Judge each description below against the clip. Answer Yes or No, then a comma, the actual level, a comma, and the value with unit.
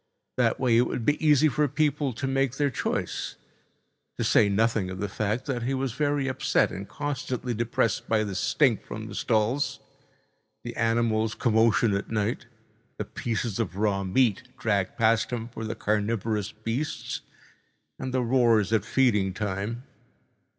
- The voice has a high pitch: No, low, 115 Hz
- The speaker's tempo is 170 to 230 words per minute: No, average, 160 wpm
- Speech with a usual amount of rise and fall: Yes, average, 3.5 semitones